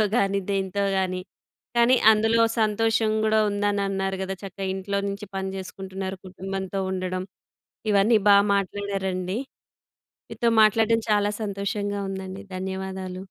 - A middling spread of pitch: No, narrow, 1.4 semitones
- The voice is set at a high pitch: Yes, high, 195 Hz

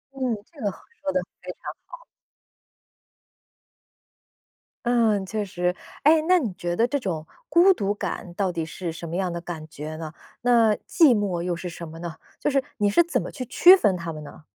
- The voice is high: Yes, high, 195 Hz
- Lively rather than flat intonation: Yes, wide, 6.8 semitones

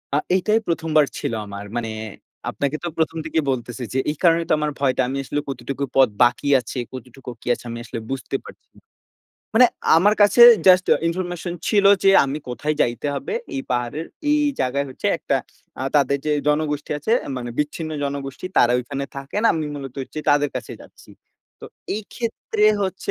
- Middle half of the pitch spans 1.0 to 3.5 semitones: No, average, 4.5 semitones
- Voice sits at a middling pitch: Yes, medium, 145 Hz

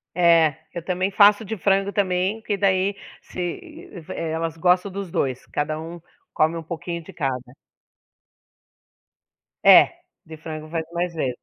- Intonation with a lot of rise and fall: No, average, 3.4 semitones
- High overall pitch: No, medium, 170 Hz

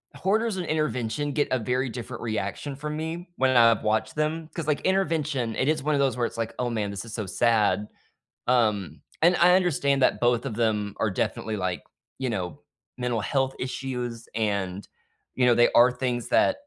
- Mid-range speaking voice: No, low, 125 Hz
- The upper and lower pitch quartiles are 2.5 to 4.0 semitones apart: No, average, 5.1 semitones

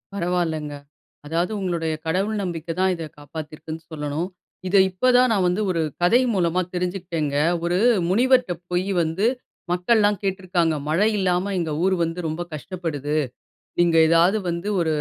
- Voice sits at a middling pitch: Yes, medium, 175 Hz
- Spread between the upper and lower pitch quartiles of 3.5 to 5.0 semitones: No, average, 2.7 semitones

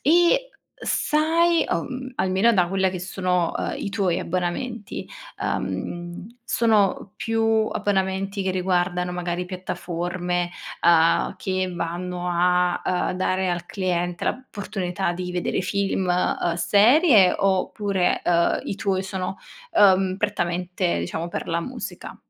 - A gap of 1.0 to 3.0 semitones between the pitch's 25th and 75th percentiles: Yes, narrow, 2.4 semitones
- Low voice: No, medium, 185 Hz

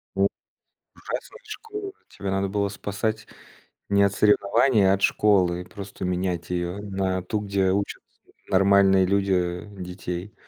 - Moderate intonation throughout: No, narrow, 1.7 semitones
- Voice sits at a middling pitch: No, very low, 95 Hz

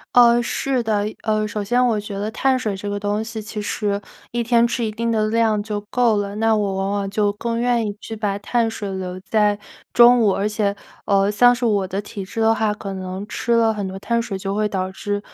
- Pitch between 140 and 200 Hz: No, high, 210 Hz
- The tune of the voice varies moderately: No, narrow, 2.3 semitones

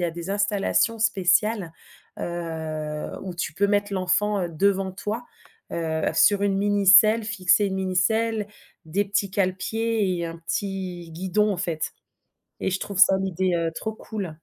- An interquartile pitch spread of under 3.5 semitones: Yes, average, 2.9 semitones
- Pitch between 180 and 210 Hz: Yes, high, 190 Hz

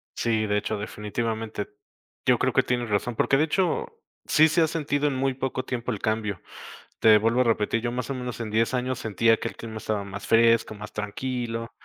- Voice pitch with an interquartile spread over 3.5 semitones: No, average, 2.9 semitones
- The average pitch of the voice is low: Yes, low, 115 Hz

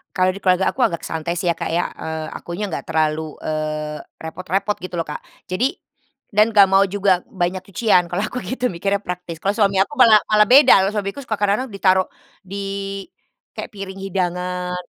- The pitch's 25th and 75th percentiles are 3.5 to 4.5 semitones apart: No, average, 2.9 semitones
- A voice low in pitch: No, high, 190 Hz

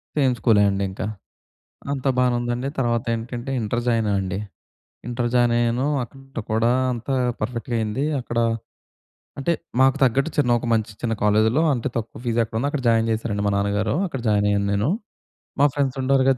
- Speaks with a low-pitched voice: Yes, low, 120 Hz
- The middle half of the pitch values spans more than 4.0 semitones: No, average, 3.2 semitones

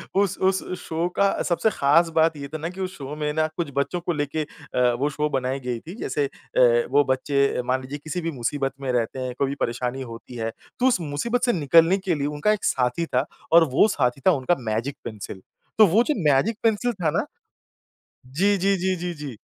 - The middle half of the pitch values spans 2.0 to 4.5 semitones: No, average, 5.2 semitones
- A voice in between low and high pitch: Yes, medium, 150 Hz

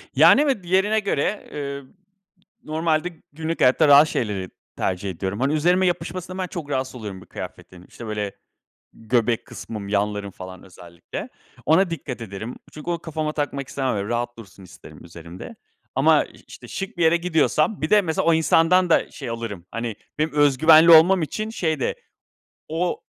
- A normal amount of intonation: No, wide, 7.7 semitones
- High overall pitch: No, medium, 145 Hz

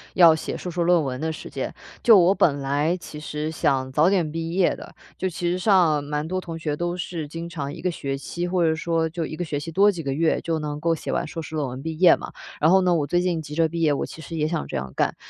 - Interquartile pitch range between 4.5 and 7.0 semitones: No, narrow, 2.5 semitones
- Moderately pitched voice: Yes, medium, 165 Hz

